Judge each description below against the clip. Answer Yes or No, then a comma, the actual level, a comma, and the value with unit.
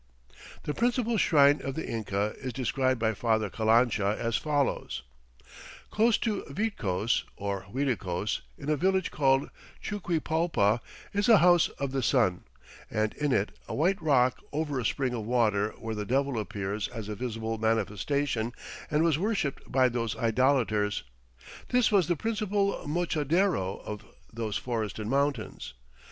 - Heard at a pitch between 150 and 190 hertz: No, low, 130 Hz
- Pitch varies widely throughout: Yes, wide, 6.3 semitones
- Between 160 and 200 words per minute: No, average, 145 wpm